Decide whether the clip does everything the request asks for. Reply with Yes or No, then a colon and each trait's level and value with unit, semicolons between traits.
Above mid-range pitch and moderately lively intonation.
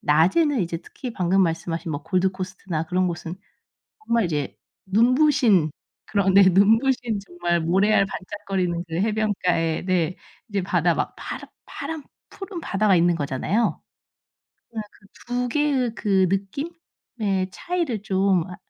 Yes: high, 195 Hz; average, 4.5 semitones